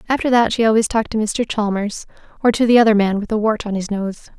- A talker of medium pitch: No, high, 220 Hz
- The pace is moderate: No, fast, 260 wpm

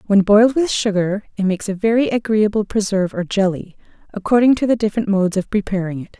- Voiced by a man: No, female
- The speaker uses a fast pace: No, average, 195 wpm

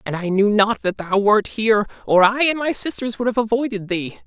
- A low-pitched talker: No, high, 215 Hz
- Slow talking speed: No, fast, 240 wpm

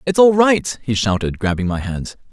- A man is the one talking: Yes, male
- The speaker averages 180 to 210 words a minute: Yes, fast, 205 wpm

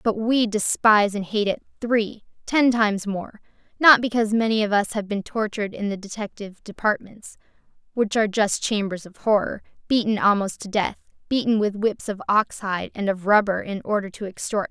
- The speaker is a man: No, female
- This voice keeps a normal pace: No, fast, 215 wpm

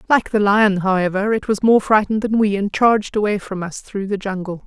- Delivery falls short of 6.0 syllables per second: Yes, 5.6 syllables/s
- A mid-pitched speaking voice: No, high, 205 Hz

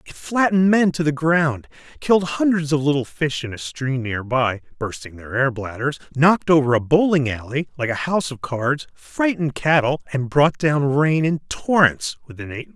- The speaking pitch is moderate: Yes, medium, 145 Hz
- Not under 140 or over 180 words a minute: No, average, 195 wpm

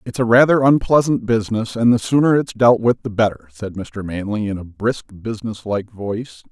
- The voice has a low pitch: Yes, low, 115 Hz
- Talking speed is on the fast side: No, average, 195 wpm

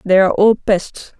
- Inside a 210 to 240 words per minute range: No, average, 200 wpm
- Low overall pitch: No, high, 195 Hz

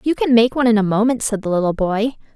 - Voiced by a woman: Yes, female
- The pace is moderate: No, fast, 280 wpm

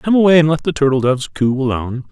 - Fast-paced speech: Yes, fast, 255 wpm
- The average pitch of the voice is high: No, medium, 145 Hz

